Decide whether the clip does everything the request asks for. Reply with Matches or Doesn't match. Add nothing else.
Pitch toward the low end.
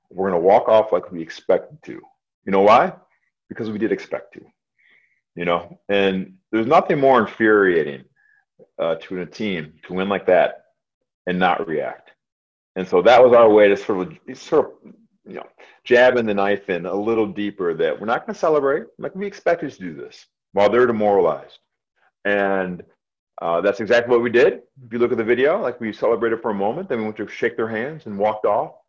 Matches